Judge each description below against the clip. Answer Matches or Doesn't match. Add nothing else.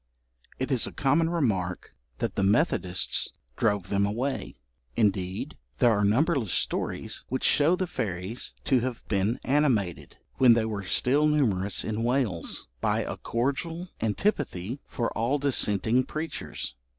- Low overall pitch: Matches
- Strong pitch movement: Matches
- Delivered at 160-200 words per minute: Doesn't match